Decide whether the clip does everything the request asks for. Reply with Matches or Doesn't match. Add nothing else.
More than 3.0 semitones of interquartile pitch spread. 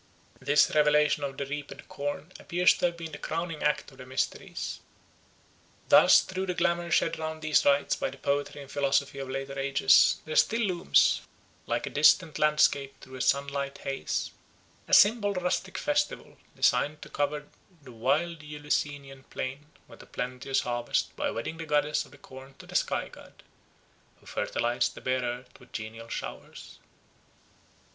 Doesn't match